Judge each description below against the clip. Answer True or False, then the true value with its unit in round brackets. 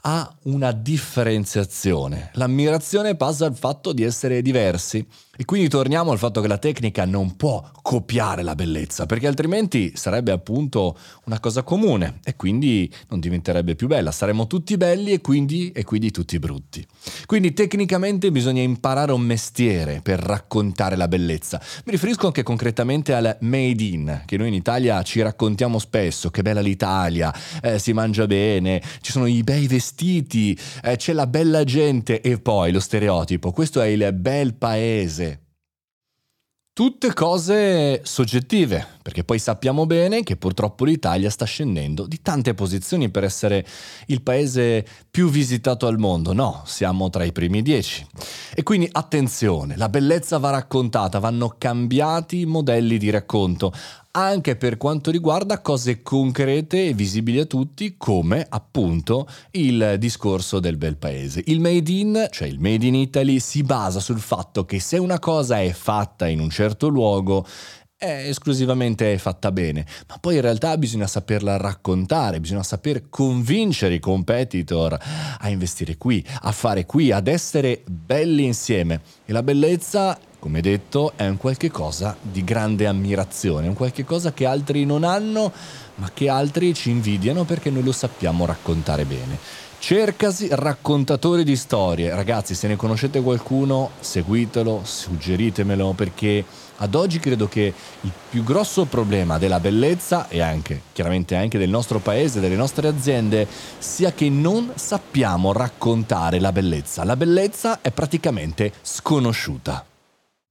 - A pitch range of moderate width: False (6.9 semitones)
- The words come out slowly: False (150 wpm)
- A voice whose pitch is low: True (120 Hz)